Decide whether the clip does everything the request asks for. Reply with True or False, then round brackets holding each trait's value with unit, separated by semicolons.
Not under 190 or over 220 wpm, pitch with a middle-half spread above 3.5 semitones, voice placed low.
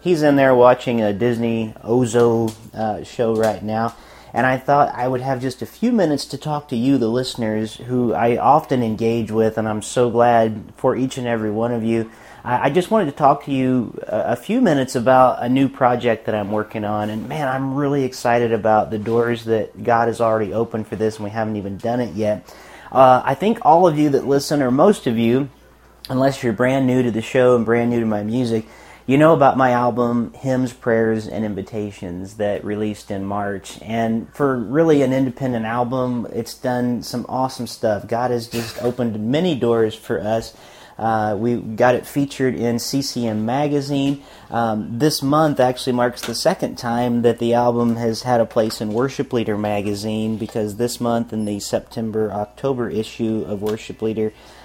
False (200 wpm; 2.7 semitones; 120 Hz)